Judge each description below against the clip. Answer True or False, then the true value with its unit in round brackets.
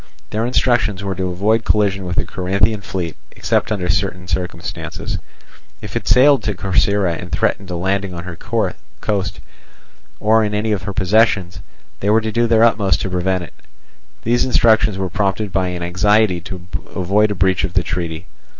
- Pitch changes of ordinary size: True (3.0 semitones)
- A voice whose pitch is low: True (95 Hz)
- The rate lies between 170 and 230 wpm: True (175 wpm)